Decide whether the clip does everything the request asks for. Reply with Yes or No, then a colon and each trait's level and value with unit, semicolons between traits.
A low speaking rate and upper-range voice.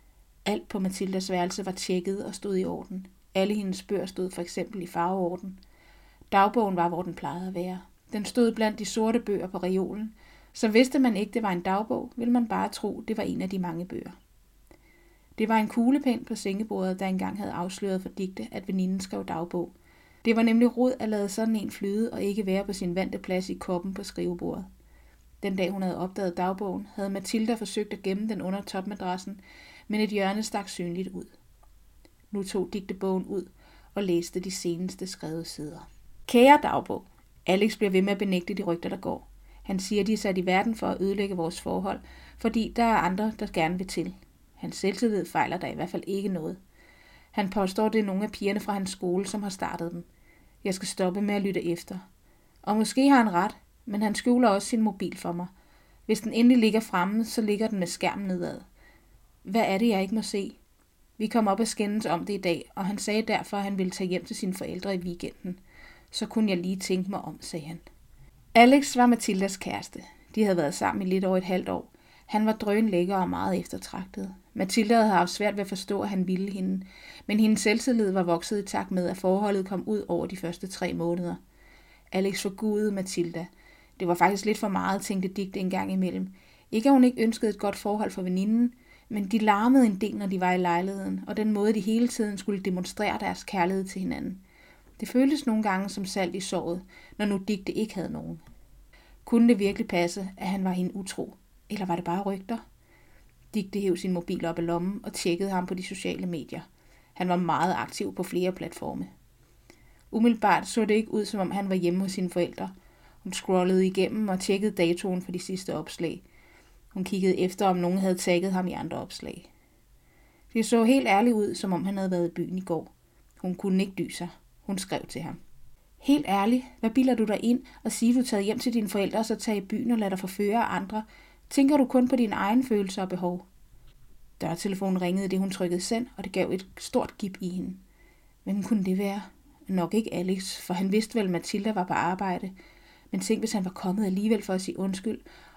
No: average, 215 wpm; high, 195 Hz